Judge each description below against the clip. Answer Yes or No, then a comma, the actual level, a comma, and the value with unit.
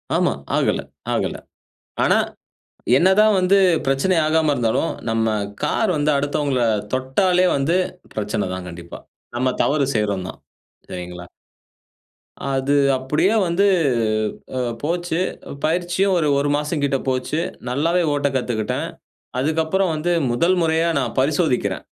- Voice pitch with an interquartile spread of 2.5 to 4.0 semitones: No, average, 5.0 semitones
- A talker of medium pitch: Yes, medium, 145 Hz